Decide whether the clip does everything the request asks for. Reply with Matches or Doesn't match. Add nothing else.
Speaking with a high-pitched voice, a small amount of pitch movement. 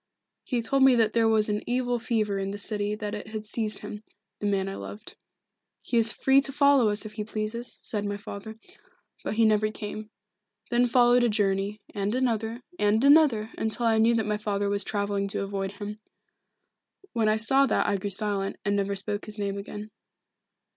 Matches